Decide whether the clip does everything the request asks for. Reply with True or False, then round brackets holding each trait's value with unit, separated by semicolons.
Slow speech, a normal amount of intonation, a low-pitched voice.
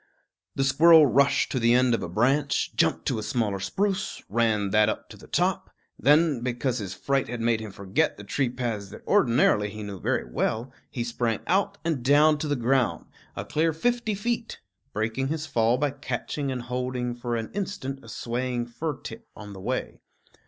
False (195 wpm; 4.3 semitones; 125 Hz)